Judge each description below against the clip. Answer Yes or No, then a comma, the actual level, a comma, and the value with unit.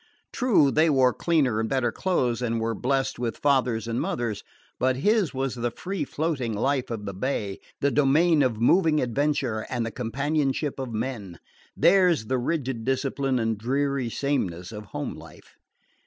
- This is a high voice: No, low, 130 Hz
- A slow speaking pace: No, average, 165 wpm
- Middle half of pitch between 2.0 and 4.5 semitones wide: Yes, average, 4.0 semitones